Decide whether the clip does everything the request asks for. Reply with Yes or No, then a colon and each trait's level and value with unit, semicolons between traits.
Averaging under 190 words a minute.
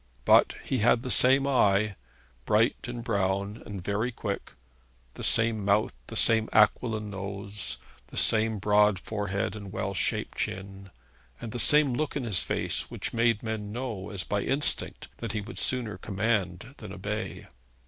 Yes: average, 160 wpm